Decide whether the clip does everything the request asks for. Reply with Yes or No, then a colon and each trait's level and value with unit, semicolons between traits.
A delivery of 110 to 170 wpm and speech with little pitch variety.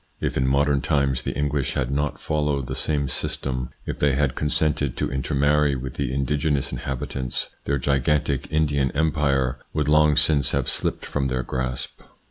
Yes: average, 165 wpm; narrow, 1.9 semitones